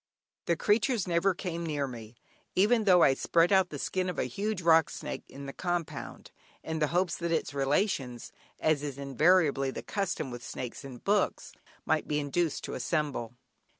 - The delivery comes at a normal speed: Yes, average, 180 wpm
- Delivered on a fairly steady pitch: No, average, 4.9 semitones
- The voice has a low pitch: No, medium, 160 Hz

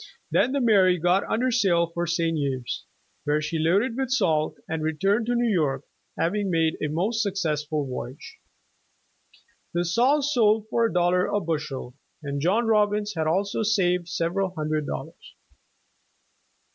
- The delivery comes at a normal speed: Yes, average, 160 wpm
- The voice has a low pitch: No, medium, 180 Hz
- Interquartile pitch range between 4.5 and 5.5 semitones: Yes, average, 5.2 semitones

